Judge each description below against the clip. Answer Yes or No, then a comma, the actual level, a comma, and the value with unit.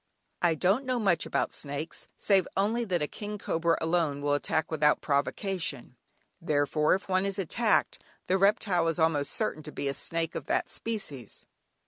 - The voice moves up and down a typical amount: Yes, average, 4.8 semitones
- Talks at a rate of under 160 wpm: No, average, 170 wpm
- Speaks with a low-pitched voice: No, medium, 165 Hz